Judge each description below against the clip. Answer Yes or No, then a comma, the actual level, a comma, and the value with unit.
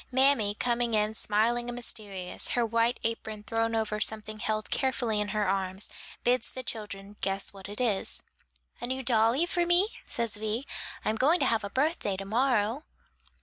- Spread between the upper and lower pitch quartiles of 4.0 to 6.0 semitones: No, average, 2.9 semitones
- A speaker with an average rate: Yes, average, 175 wpm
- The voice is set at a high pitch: Yes, high, 225 Hz